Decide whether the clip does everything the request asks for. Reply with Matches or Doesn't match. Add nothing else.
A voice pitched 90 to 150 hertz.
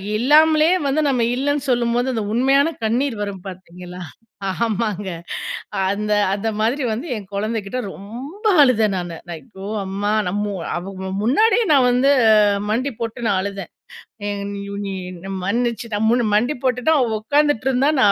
Doesn't match